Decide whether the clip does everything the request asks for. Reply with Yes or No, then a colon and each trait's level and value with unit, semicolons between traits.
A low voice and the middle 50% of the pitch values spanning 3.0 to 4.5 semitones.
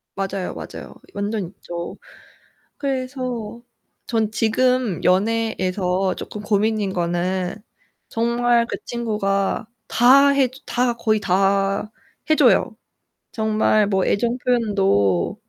No: high, 215 Hz; average, 3.6 semitones